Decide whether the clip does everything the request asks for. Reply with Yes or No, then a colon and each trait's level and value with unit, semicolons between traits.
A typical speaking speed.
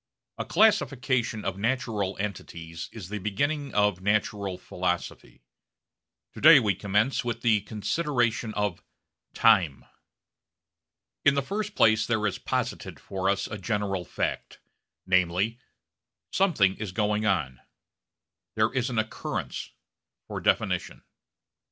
No: slow, 120 wpm